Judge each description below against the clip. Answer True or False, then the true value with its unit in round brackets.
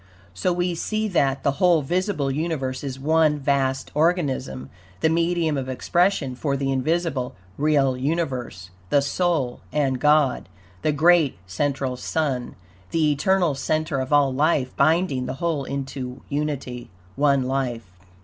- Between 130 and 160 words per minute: True (140 wpm)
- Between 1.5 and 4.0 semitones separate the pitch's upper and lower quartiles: True (3.5 semitones)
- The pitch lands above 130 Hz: True (140 Hz)